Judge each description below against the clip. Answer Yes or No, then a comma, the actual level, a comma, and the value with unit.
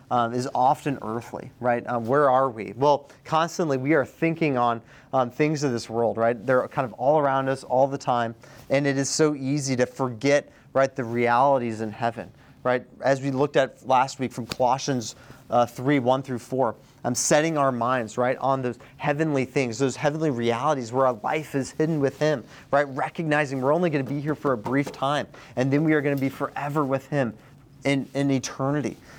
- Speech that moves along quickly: Yes, fast, 210 wpm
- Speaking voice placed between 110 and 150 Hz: Yes, low, 135 Hz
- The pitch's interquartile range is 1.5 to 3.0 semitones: Yes, narrow, 2.5 semitones